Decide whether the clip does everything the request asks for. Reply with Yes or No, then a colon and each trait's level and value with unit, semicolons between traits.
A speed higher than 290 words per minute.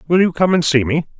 Yes: fast, 300 wpm